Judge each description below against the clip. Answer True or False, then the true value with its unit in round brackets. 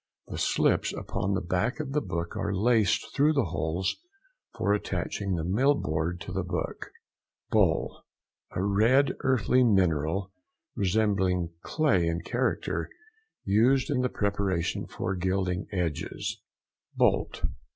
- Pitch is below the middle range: True (95 Hz)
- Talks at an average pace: False (125 wpm)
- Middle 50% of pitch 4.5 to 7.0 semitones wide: True (4.9 semitones)